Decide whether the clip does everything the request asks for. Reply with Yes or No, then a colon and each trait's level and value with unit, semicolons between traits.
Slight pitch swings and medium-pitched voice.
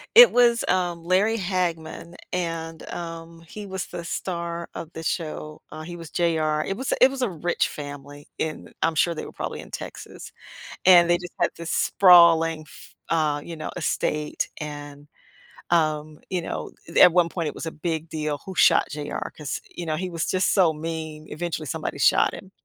Yes: narrow, 2.2 semitones; medium, 165 Hz